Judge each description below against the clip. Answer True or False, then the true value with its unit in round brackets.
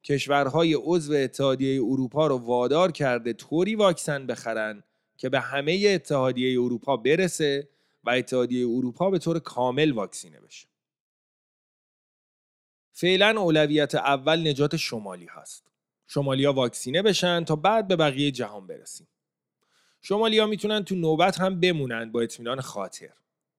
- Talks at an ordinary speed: True (135 wpm)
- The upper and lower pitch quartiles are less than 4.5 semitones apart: False (5.3 semitones)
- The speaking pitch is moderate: True (145 Hz)